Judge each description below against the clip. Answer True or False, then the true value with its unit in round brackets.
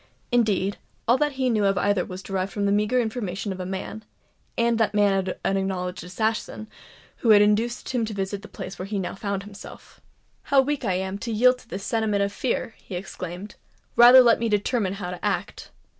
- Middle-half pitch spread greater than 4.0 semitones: False (3.2 semitones)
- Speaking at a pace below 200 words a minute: False (205 wpm)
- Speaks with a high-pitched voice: True (205 Hz)